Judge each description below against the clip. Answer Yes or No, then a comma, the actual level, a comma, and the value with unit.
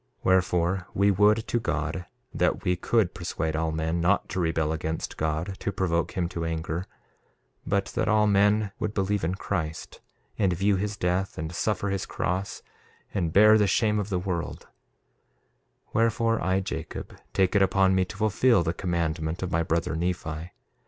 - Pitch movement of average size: Yes, average, 3.4 semitones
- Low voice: Yes, very low, 95 Hz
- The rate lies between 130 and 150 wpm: No, average, 170 wpm